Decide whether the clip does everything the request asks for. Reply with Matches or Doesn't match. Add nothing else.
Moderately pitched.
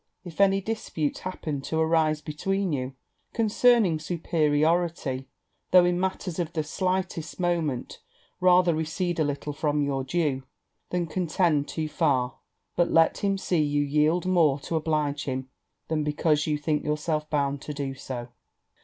Matches